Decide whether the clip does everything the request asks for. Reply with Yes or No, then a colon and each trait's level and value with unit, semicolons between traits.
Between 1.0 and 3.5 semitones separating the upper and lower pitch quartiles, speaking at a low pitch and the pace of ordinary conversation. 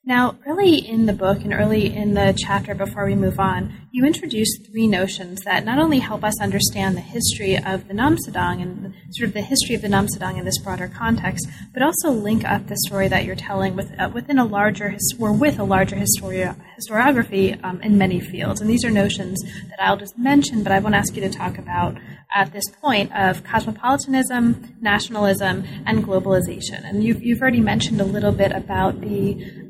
No: average, 3.2 semitones; high, 205 Hz; average, 195 wpm